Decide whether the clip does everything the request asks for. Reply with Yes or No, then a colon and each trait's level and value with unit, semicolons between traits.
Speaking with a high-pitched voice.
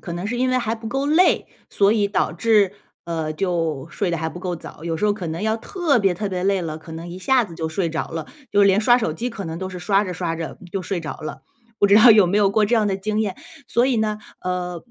Yes: high, 195 Hz